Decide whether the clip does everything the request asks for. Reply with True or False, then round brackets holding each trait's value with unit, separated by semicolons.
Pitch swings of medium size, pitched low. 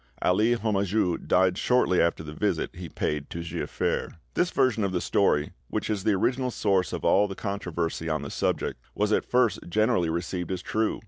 True (4.2 semitones; 95 Hz)